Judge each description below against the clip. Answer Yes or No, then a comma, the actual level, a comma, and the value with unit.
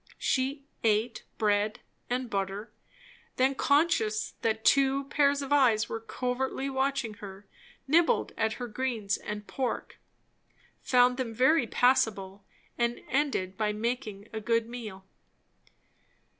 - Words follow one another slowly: Yes, slow, 120 wpm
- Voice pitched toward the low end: No, high, 235 Hz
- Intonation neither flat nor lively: Yes, average, 3.9 semitones